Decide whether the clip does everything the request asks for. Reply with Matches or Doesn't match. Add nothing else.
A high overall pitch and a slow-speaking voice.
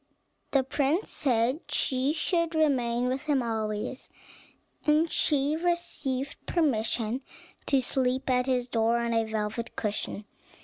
Matches